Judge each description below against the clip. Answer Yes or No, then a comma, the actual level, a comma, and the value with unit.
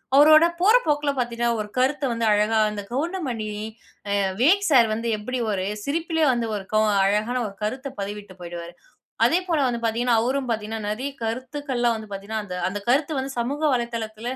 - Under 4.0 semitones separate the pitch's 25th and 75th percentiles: No, average, 4.7 semitones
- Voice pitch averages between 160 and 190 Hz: No, high, 235 Hz